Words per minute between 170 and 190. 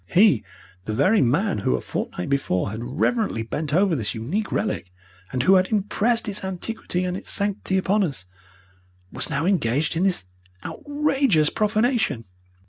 No: average, 155 wpm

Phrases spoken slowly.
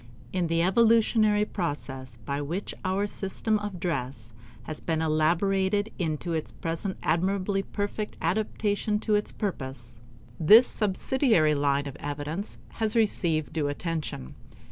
Yes: slow, 125 wpm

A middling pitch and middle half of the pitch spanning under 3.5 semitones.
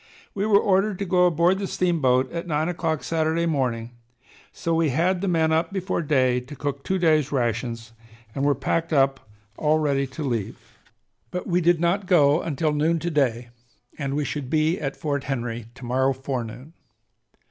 No: medium, 150 Hz; average, 4.2 semitones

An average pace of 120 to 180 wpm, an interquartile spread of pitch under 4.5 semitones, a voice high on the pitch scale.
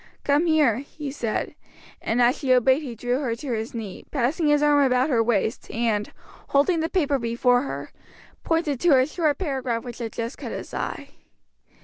No: average, 190 wpm; average, 3.9 semitones; very high, 260 Hz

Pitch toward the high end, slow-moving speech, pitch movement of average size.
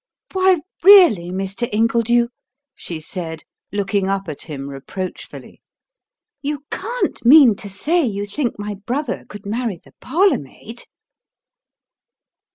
No: high, 215 Hz; slow, 120 wpm; wide, 6.7 semitones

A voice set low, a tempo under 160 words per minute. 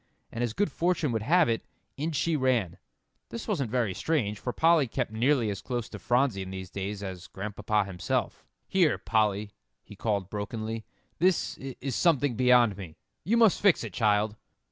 No: low, 115 Hz; average, 175 wpm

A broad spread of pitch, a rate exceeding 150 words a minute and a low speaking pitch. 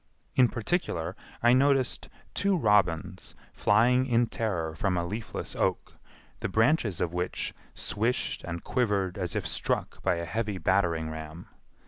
No: wide, 5.7 semitones; average, 140 wpm; low, 100 Hz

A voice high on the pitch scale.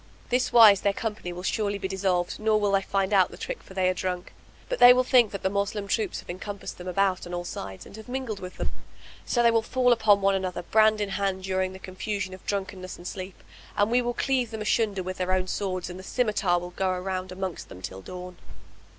Yes: high, 195 Hz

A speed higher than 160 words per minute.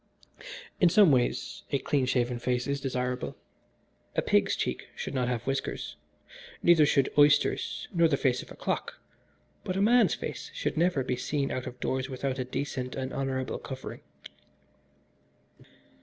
No: average, 155 wpm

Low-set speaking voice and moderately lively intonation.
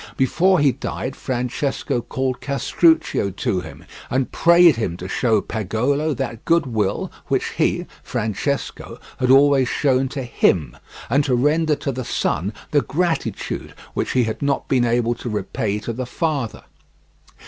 Yes: low, 130 Hz; average, 3.9 semitones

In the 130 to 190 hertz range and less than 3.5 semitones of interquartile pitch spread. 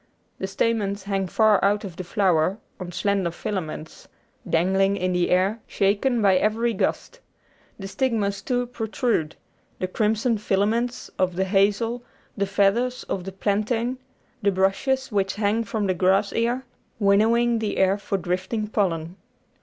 No: high, 200 Hz; average, 2.9 semitones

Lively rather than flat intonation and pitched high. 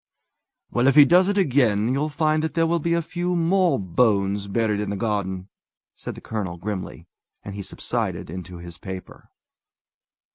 No: wide, 8.5 semitones; low, 110 Hz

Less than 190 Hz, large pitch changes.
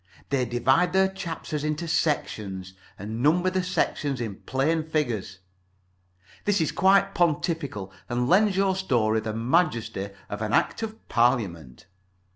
Yes: medium, 140 Hz; wide, 8.1 semitones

